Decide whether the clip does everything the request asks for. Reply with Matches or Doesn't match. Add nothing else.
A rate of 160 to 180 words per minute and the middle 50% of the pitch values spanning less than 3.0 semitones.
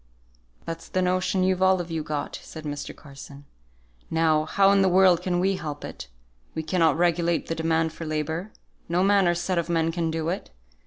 Doesn't match